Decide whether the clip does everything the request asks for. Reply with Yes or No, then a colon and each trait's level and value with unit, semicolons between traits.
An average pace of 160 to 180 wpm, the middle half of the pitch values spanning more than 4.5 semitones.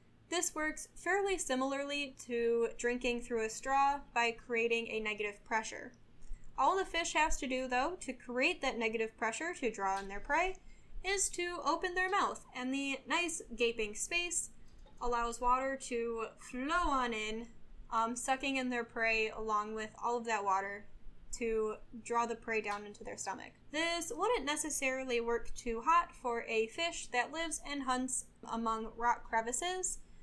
Yes: average, 165 wpm; wide, 5.4 semitones